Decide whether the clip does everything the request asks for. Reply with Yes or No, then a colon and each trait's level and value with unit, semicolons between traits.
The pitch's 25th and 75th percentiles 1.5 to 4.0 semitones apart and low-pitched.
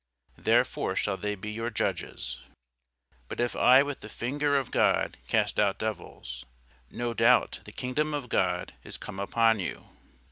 Yes: average, 3.5 semitones; low, 115 Hz